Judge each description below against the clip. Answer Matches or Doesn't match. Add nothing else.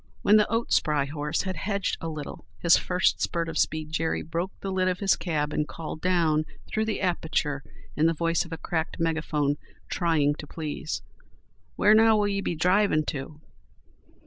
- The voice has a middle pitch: Matches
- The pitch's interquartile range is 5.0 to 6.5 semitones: Doesn't match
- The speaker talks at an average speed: Matches